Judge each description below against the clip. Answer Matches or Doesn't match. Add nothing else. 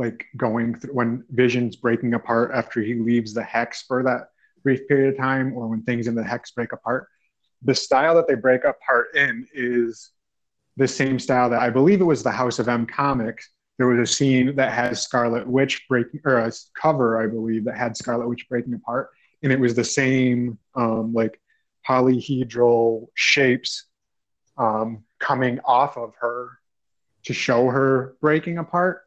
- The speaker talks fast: Doesn't match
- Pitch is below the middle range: Matches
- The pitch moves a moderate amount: Doesn't match